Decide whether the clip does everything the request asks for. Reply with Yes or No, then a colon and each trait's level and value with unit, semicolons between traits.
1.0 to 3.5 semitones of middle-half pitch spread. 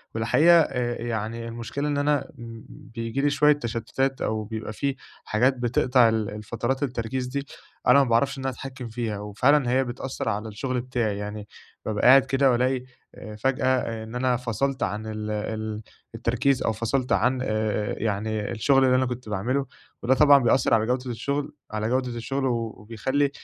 Yes: average, 3.2 semitones